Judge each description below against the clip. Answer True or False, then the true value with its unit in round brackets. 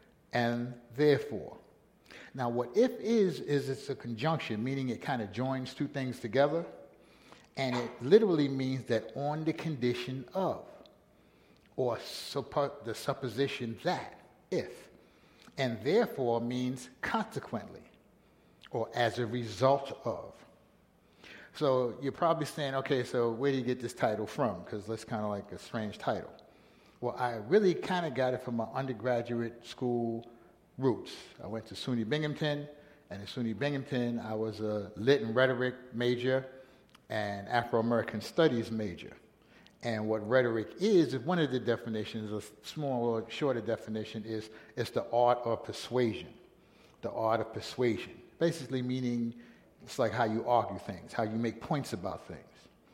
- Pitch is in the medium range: False (120 Hz)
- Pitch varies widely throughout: False (3.2 semitones)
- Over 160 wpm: False (150 wpm)